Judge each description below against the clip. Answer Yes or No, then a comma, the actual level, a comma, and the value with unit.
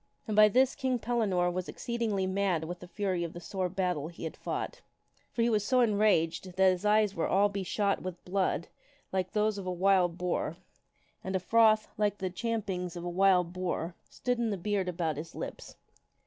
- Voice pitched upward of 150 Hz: Yes, high, 190 Hz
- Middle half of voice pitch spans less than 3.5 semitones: Yes, average, 3.0 semitones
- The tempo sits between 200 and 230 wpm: Yes, fast, 205 wpm